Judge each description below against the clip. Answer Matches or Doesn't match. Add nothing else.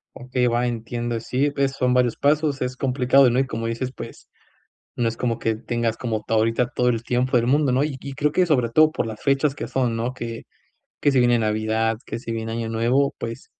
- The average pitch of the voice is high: Doesn't match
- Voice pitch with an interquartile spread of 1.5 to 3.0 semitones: Matches